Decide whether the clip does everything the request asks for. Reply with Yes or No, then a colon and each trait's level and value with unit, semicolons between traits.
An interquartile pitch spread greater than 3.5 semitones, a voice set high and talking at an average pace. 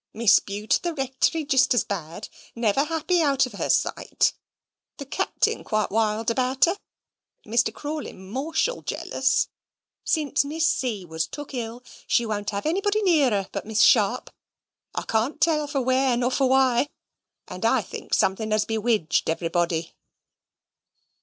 Yes: wide, 5.4 semitones; high, 245 Hz; average, 155 wpm